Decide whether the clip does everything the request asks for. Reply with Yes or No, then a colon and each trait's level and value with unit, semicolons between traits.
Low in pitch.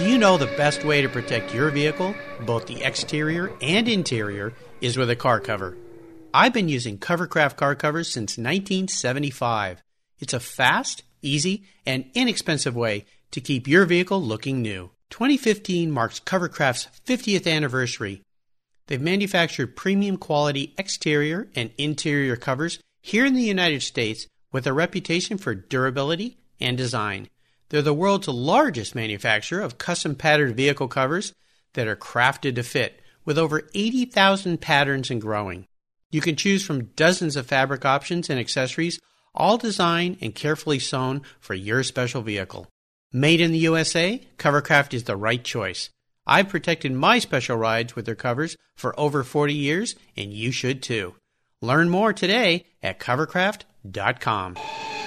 No: medium, 145 Hz